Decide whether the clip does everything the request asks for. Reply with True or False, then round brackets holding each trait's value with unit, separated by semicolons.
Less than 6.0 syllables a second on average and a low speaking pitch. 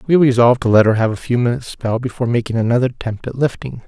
False (7.3 syllables/s; 120 Hz)